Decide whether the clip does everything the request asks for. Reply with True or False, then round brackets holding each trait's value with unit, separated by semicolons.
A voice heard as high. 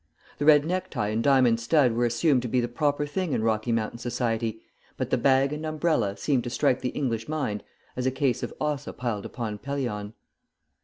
False (125 Hz)